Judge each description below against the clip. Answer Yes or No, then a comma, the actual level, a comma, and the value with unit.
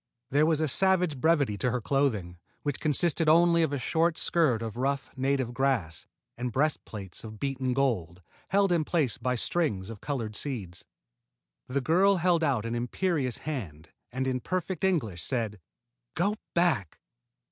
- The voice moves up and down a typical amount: No, wide, 6.1 semitones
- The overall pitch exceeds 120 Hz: Yes, low, 135 Hz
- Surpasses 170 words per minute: No, average, 160 wpm